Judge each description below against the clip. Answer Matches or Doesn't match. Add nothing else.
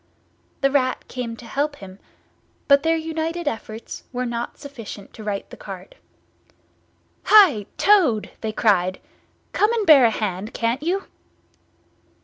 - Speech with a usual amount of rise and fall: Doesn't match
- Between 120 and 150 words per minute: Matches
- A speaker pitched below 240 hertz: Doesn't match